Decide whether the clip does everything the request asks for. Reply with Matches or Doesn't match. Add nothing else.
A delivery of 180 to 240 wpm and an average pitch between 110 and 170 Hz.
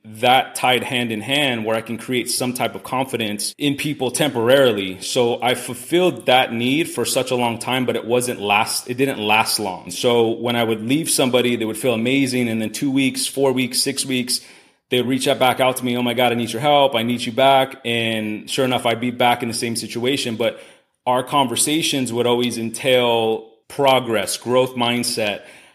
Matches